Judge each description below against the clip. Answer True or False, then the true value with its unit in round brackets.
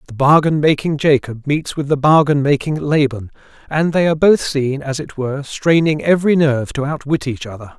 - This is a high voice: False (145 Hz)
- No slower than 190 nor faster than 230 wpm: True (195 wpm)